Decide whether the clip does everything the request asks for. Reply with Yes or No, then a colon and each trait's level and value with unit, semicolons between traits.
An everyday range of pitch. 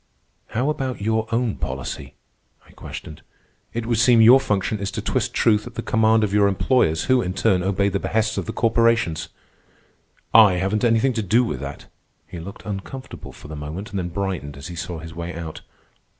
Yes: average, 4.7 semitones